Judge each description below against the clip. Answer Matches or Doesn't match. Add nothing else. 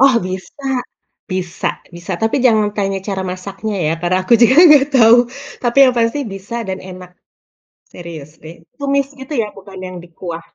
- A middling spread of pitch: Matches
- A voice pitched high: Matches